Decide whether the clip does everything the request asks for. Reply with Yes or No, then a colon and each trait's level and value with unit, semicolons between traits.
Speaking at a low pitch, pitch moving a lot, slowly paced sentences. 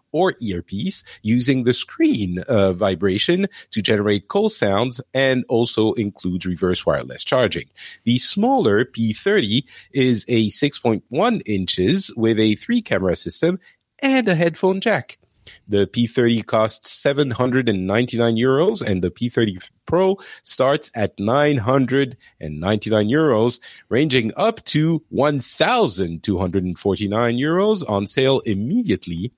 Yes: low, 120 Hz; wide, 6.4 semitones; slow, 110 wpm